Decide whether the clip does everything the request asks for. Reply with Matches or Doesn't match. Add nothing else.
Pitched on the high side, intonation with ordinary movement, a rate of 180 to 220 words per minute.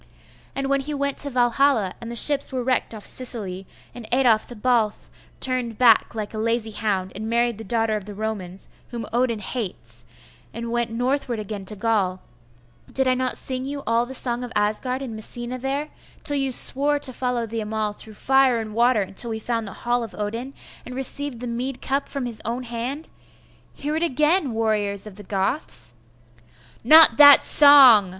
Matches